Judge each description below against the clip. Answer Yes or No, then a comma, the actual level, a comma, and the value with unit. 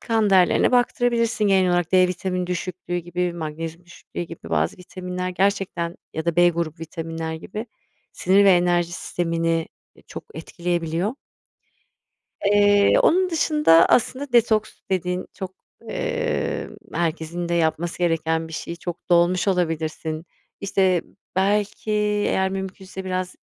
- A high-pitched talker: No, medium, 180 Hz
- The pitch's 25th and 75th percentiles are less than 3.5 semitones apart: Yes, average, 2.7 semitones